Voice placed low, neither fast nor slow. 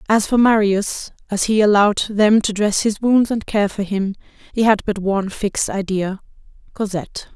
No: high, 205 Hz; average, 180 wpm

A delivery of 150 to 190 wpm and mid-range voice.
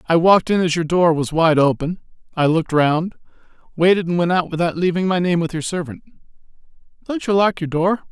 No: fast, 205 wpm; medium, 170 Hz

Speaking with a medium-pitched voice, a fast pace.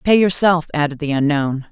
No: medium, 155 Hz; average, 175 wpm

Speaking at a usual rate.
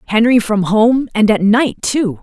Yes: average, 190 wpm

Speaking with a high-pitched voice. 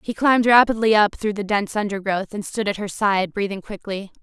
Yes: high, 205 Hz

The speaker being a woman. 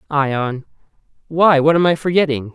No: male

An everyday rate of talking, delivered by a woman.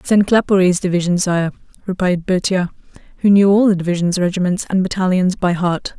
Yes: average, 160 wpm; female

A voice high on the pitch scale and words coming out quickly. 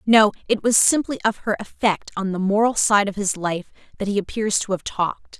Yes: high, 205 Hz; fast, 220 wpm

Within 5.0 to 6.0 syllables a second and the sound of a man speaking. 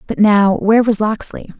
No: 5.1 syllables/s; female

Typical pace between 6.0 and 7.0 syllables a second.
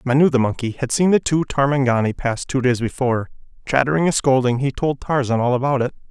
Yes: 6.1 syllables/s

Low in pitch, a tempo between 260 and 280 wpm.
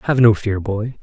No: low, 110 Hz; fast, 235 wpm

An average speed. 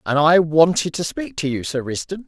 No: fast, 235 wpm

